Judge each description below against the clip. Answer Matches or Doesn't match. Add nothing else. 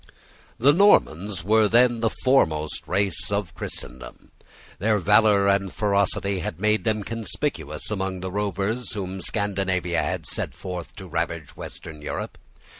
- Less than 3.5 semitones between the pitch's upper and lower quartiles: Matches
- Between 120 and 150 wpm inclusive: Matches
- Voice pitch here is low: Matches